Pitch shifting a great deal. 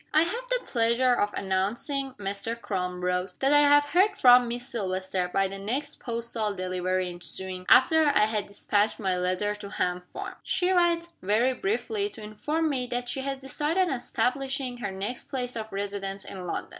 Yes: wide, 6.0 semitones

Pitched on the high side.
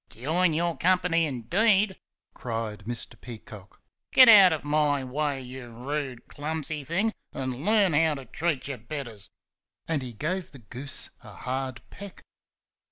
No: medium, 145 Hz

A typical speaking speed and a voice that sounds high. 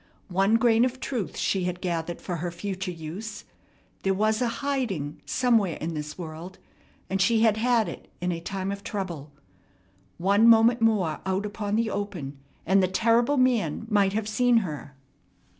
Yes: average, 170 wpm; high, 200 Hz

